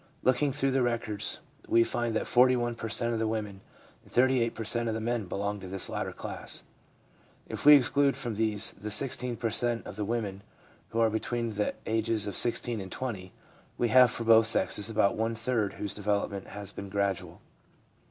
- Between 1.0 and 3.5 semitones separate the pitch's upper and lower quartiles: Yes, narrow, 2.6 semitones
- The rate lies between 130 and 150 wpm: No, average, 195 wpm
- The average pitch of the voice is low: Yes, low, 115 Hz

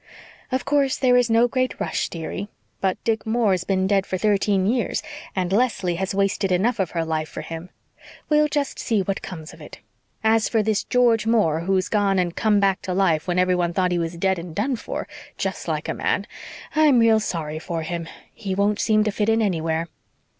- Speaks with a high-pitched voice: Yes, high, 195 Hz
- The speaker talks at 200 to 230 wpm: Yes, fast, 205 wpm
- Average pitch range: Yes, average, 4.0 semitones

